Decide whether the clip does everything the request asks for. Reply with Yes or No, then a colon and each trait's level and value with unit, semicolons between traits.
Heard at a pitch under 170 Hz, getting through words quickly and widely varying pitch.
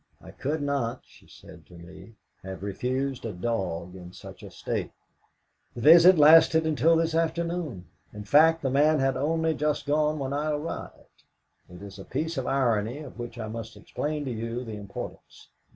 No: low, 135 Hz; average, 180 wpm; wide, 6.0 semitones